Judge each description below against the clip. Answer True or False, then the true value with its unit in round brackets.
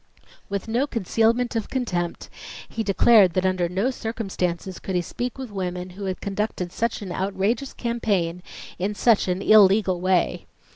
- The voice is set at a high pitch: True (195 Hz)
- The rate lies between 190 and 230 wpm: False (155 wpm)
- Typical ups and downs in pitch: True (3.7 semitones)